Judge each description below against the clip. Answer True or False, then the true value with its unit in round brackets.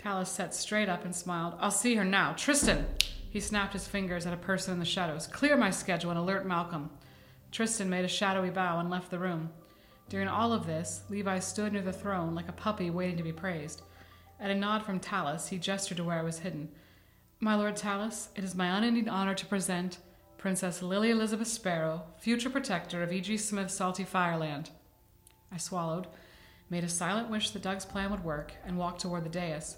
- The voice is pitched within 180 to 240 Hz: True (185 Hz)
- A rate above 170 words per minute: True (205 wpm)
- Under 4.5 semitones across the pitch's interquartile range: True (2.8 semitones)